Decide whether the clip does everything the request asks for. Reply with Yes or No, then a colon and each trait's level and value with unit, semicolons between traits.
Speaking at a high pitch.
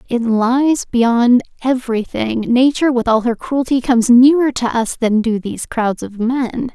Yes: high, 240 Hz